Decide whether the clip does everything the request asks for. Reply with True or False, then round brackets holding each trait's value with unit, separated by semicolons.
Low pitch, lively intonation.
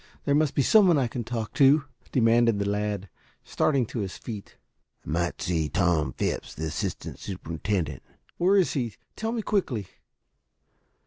True (110 Hz; 7.5 semitones)